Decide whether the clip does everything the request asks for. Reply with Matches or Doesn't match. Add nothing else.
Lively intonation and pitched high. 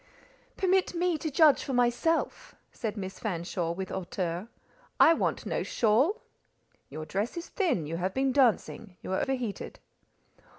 Matches